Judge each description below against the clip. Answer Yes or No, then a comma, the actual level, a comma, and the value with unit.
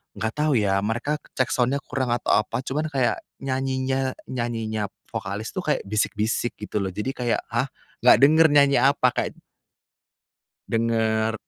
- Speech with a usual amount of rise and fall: Yes, average, 3.4 semitones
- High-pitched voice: No, low, 120 Hz